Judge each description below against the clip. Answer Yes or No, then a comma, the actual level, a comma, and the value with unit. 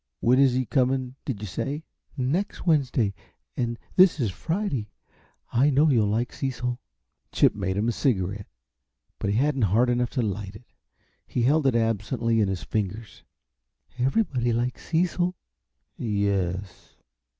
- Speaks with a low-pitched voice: Yes, low, 120 Hz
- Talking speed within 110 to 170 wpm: Yes, average, 145 wpm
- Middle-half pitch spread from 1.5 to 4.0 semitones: No, average, 4.4 semitones